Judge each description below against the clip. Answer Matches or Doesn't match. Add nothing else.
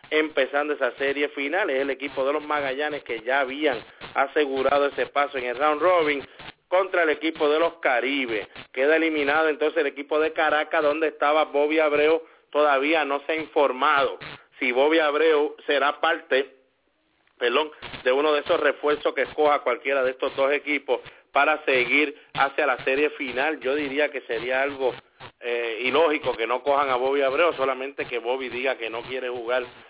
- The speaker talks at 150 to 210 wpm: Matches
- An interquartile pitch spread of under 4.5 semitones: Matches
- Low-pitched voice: Doesn't match